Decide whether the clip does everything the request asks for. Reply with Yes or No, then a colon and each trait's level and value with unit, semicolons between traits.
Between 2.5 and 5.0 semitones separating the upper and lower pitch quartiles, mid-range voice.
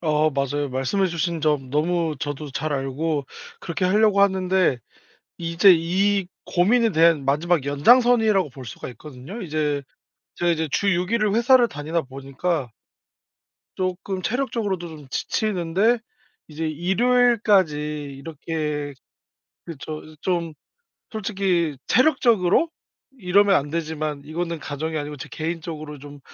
Yes: average, 4.6 semitones; medium, 165 Hz